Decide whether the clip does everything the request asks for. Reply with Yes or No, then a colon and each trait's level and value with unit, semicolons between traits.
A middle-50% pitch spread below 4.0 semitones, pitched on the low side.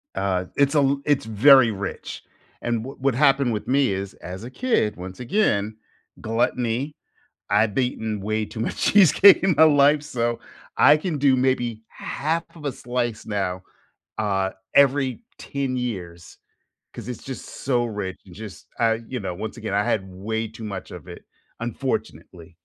No: average, 5.0 semitones; low, 115 Hz